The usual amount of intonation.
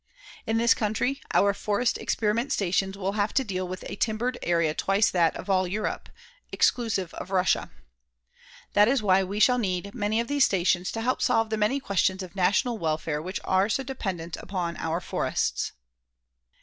Yes: average, 3.5 semitones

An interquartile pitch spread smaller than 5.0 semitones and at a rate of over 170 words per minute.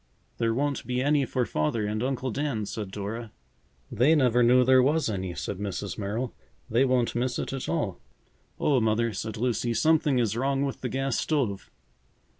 Yes: average, 3.8 semitones; average, 180 wpm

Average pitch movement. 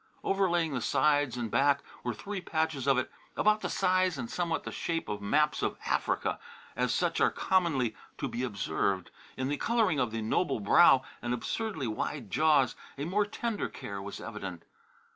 No: wide, 6.8 semitones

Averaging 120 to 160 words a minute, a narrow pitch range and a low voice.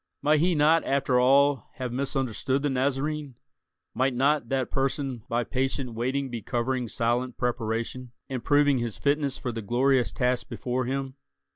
Yes: average, 155 wpm; narrow, 2.3 semitones; low, 130 Hz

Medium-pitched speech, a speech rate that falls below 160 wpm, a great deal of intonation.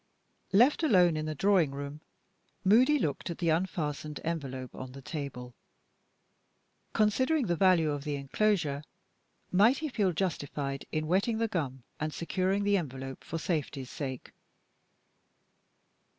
Yes: medium, 165 Hz; slow, 135 wpm; wide, 5.7 semitones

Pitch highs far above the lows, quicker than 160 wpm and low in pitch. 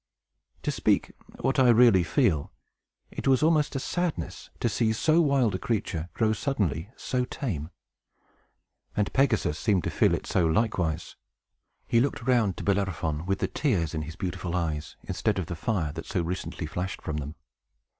Yes: wide, 6.9 semitones; average, 170 wpm; low, 100 Hz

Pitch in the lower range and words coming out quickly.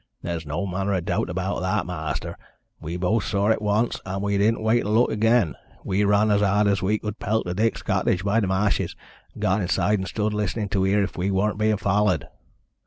Yes: low, 100 Hz; fast, 220 wpm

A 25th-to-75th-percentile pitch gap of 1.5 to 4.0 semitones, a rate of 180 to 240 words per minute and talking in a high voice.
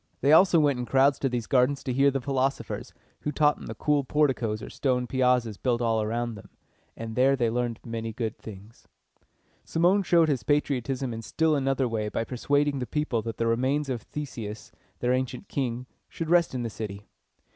No: average, 3.7 semitones; average, 195 wpm; low, 125 Hz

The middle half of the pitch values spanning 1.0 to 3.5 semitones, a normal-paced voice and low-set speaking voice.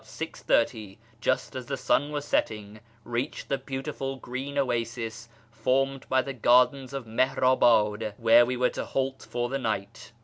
Yes: average, 2.8 semitones; average, 150 wpm; low, 125 Hz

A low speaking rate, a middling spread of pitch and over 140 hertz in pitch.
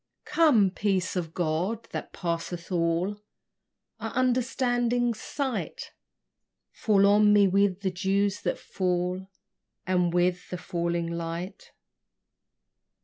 Yes: slow, 105 wpm; average, 3.1 semitones; high, 190 Hz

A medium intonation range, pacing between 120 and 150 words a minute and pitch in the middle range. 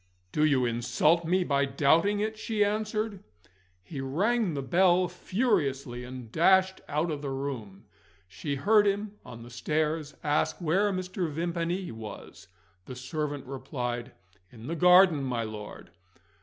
No: wide, 6.0 semitones; average, 140 wpm; medium, 155 Hz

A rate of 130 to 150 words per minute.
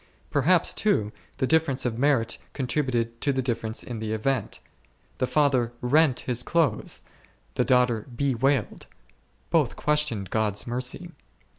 Yes: slow, 135 wpm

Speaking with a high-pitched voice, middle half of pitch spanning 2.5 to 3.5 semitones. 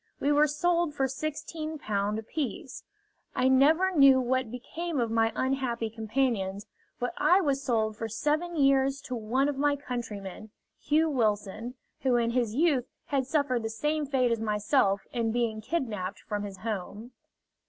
No: very high, 255 Hz; average, 4.5 semitones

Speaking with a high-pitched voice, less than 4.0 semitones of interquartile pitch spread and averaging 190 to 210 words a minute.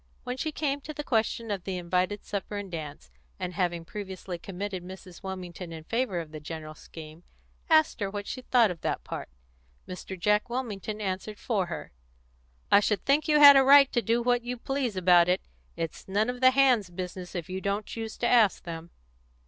No: high, 200 Hz; average, 5.3 semitones; average, 200 wpm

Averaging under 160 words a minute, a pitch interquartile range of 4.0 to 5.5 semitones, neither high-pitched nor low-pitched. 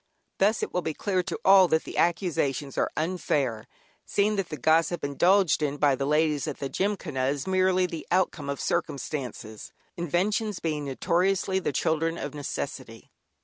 No: average, 165 wpm; average, 4.6 semitones; medium, 165 Hz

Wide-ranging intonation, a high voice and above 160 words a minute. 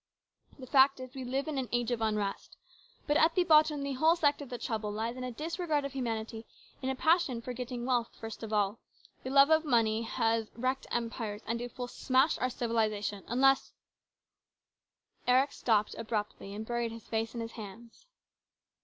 No: average, 3.3 semitones; high, 245 Hz; average, 190 wpm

